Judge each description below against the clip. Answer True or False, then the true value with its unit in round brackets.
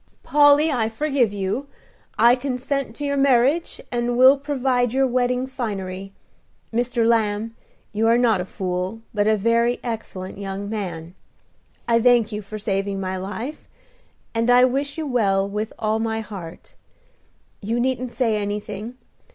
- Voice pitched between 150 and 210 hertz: False (230 Hz)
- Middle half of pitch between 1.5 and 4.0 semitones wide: True (3.5 semitones)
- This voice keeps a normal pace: True (150 wpm)